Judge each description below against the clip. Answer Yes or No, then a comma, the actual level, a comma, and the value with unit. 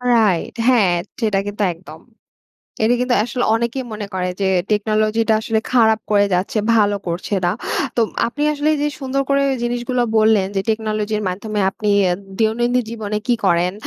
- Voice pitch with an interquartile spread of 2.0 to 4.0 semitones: Yes, average, 2.9 semitones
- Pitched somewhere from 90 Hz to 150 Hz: No, high, 220 Hz